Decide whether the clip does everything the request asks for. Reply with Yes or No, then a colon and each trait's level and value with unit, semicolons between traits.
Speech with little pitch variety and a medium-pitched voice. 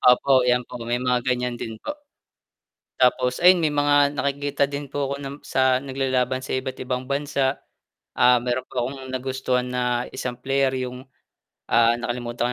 No: narrow, 1.7 semitones; low, 130 Hz